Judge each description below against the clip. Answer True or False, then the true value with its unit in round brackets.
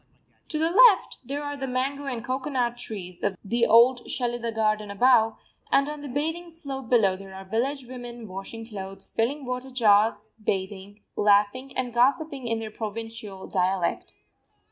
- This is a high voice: True (235 Hz)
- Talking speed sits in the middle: True (160 wpm)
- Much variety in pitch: False (4.3 semitones)